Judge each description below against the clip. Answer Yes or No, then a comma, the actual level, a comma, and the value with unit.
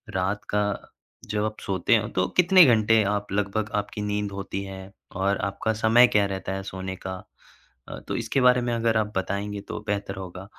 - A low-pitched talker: Yes, low, 105 Hz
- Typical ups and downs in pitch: No, narrow, 2.1 semitones